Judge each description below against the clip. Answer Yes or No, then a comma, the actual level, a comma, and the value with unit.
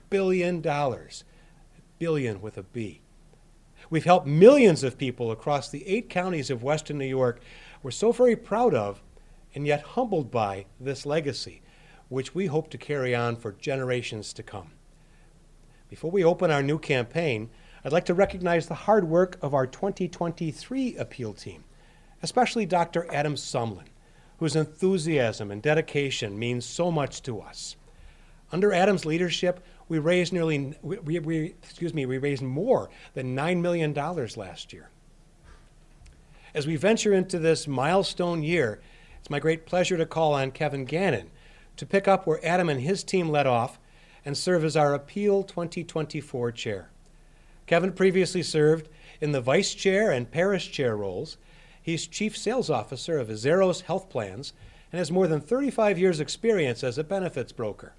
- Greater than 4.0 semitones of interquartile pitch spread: Yes, average, 4.5 semitones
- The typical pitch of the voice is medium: Yes, medium, 160 Hz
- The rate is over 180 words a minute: No, average, 155 wpm